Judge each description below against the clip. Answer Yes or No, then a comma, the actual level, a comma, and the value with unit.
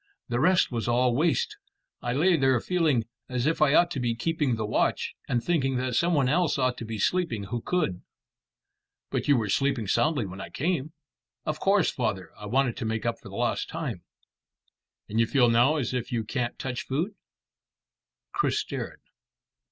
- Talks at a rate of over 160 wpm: Yes, average, 190 wpm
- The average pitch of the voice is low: Yes, low, 130 Hz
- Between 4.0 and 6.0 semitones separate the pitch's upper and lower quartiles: Yes, average, 5.1 semitones